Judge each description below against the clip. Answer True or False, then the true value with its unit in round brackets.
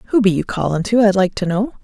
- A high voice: True (200 Hz)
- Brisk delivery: True (295 wpm)